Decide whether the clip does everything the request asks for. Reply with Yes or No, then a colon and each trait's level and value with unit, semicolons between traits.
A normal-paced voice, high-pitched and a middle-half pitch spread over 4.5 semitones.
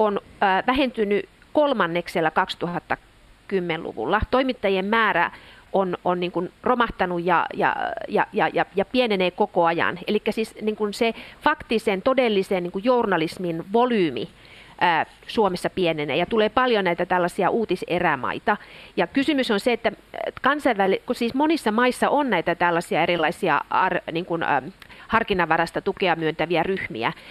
Yes: average, 125 wpm; high, 200 Hz; average, 5.3 semitones